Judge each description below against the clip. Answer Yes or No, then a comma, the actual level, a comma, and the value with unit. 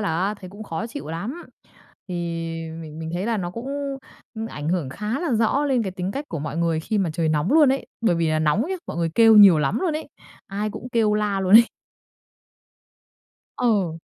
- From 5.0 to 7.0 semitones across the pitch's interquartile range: Yes, wide, 5.6 semitones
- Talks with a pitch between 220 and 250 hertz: No, high, 200 Hz